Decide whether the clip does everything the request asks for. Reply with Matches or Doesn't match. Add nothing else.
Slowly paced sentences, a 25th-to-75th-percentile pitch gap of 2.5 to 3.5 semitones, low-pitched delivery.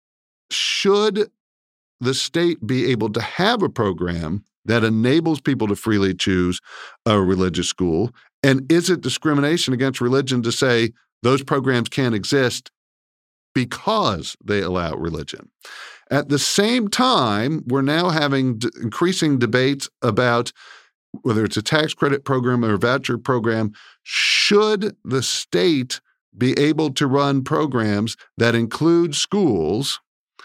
Doesn't match